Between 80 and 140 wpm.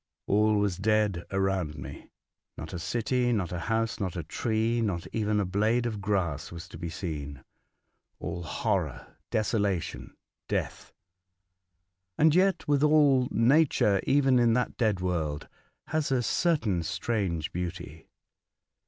Yes: slow, 135 wpm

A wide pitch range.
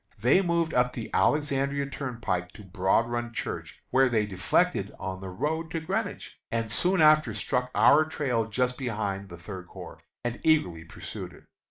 Yes: wide, 6.7 semitones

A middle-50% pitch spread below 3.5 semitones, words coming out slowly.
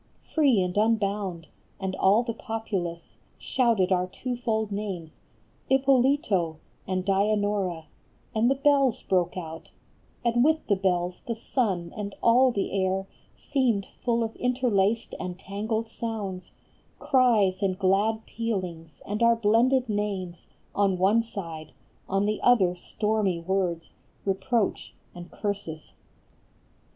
No: average, 3.8 semitones; slow, 125 wpm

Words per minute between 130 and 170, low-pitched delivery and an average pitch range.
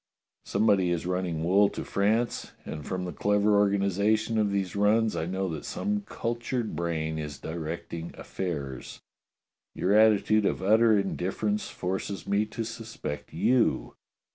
Yes: average, 140 wpm; low, 100 Hz; average, 3.7 semitones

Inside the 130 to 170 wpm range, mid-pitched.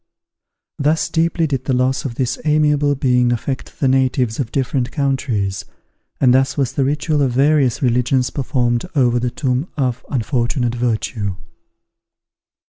No: average, 140 wpm; low, 130 Hz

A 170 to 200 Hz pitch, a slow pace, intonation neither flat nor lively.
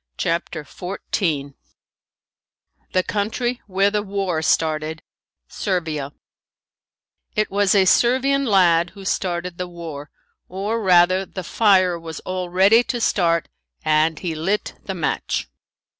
Yes: medium, 185 Hz; slow, 120 wpm; average, 3.3 semitones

